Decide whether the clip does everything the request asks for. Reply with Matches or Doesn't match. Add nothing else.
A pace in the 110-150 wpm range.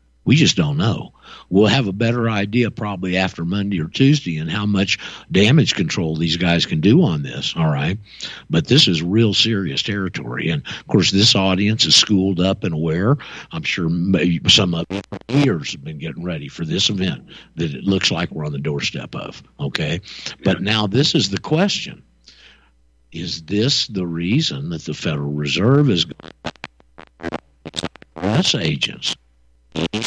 Doesn't match